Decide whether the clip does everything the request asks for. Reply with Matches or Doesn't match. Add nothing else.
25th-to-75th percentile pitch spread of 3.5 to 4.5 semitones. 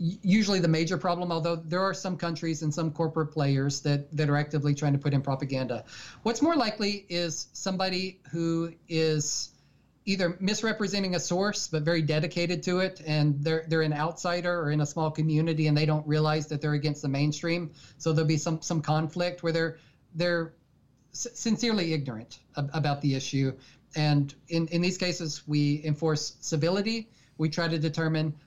Doesn't match